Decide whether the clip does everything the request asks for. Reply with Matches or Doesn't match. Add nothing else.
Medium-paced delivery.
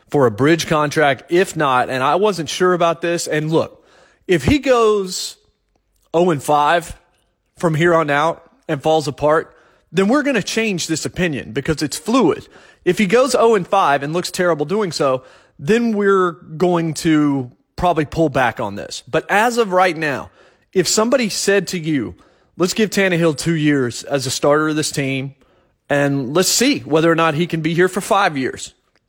Matches